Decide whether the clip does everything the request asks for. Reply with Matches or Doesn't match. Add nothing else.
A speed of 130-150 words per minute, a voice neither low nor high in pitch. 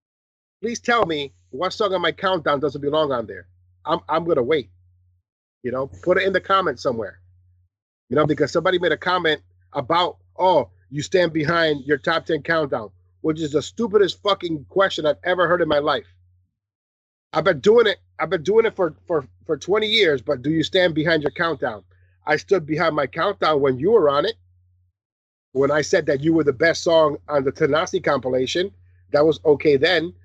Doesn't match